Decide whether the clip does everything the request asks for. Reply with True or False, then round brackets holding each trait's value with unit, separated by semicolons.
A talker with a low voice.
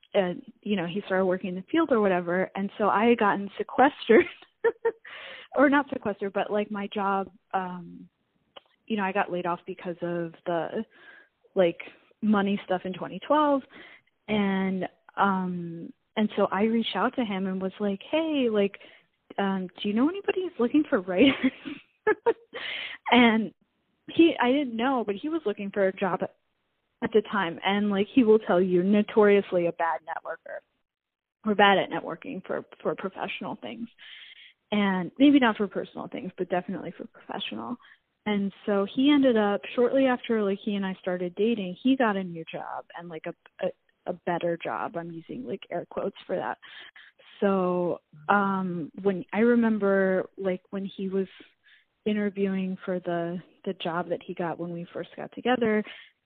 False (200 Hz)